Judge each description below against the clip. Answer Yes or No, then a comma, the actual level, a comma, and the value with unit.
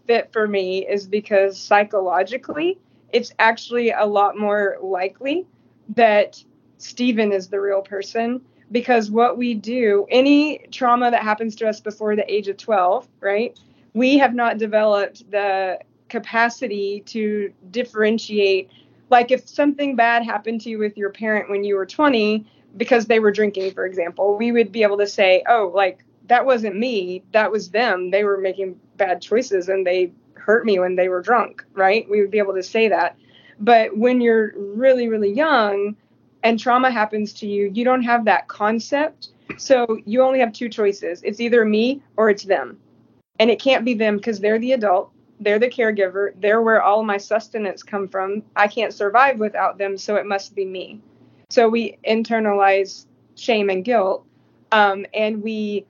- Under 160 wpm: No, average, 175 wpm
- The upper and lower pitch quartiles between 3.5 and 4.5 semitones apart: No, average, 2.8 semitones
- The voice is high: Yes, high, 215 Hz